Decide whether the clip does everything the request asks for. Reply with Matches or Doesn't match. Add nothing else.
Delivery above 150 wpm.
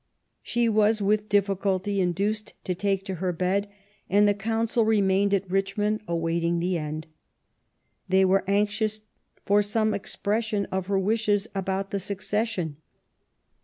Doesn't match